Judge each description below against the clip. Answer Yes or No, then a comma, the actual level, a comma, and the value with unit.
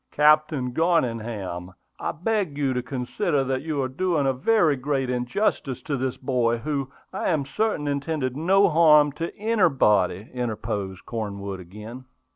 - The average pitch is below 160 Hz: Yes, low, 135 Hz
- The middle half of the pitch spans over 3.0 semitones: Yes, average, 4.5 semitones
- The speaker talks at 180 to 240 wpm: No, average, 145 wpm